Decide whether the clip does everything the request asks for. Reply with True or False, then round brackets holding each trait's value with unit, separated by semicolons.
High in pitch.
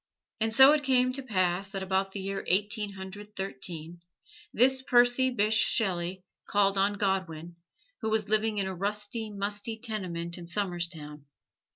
True (200 Hz)